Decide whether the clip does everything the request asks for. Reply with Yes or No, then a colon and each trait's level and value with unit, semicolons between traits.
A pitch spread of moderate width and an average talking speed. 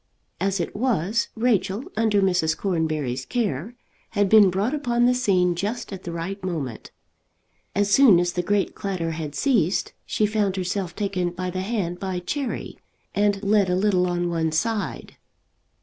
Yes: average, 3.2 semitones; average, 165 wpm